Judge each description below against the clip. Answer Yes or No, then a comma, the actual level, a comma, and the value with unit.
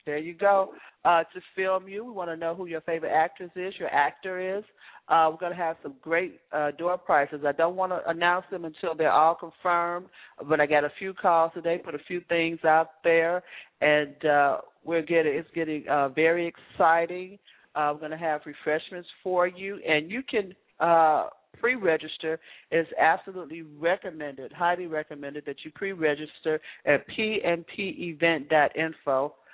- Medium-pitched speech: Yes, medium, 165 Hz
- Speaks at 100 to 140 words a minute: No, average, 165 wpm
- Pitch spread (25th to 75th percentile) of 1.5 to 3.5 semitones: Yes, narrow, 2.6 semitones